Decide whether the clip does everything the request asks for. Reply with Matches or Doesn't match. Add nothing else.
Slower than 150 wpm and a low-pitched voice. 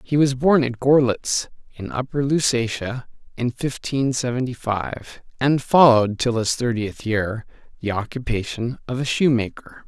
Matches